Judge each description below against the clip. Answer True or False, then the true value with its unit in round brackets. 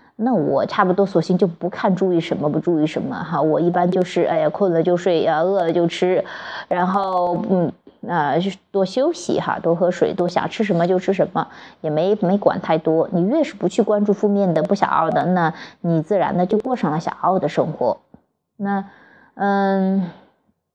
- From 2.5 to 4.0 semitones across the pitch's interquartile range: True (2.8 semitones)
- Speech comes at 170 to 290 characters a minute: True (270 characters per minute)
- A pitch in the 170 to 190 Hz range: True (185 Hz)